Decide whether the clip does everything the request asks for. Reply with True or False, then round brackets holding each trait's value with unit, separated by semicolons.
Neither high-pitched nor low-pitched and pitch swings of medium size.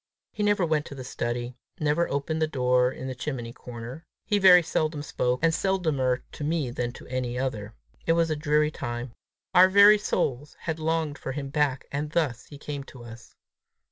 True (145 Hz; 4.3 semitones)